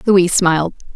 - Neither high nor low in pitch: Yes, medium, 180 Hz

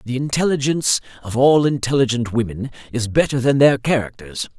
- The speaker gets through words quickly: No, average, 145 wpm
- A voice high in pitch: No, low, 125 Hz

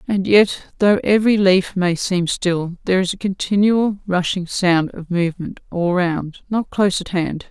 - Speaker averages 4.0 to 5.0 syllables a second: Yes, 4.6 syllables/s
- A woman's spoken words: Yes, female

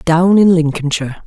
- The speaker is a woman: Yes, female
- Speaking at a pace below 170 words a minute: Yes, average, 140 wpm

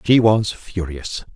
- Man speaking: Yes, male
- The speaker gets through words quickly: No, slow, 135 wpm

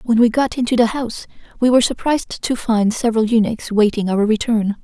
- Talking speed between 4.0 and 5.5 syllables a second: No, 5.9 syllables/s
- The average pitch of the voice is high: Yes, high, 230 Hz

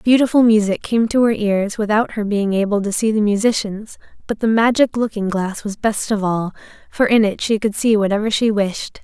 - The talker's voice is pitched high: Yes, high, 215 Hz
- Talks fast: Yes, fast, 215 wpm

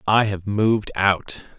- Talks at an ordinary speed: Yes, average, 150 wpm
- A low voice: Yes, low, 100 Hz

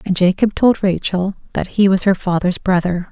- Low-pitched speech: No, high, 190 Hz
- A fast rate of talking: No, average, 195 wpm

